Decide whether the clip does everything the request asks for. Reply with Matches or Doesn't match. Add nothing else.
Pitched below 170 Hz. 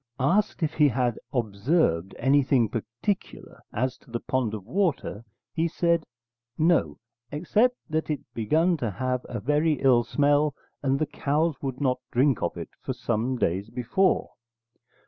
Matches